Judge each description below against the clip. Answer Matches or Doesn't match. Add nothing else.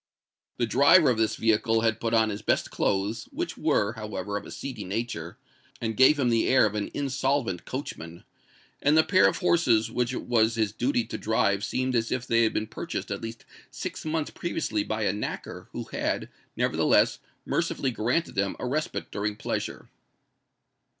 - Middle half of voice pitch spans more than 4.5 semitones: Doesn't match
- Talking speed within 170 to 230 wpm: Matches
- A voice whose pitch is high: Doesn't match